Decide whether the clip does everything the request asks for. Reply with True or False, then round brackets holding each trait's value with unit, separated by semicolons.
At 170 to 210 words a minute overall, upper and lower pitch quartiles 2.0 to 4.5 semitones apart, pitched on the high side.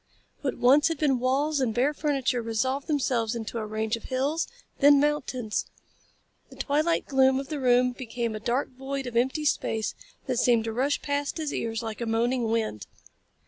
True (185 wpm; 3.6 semitones; 255 Hz)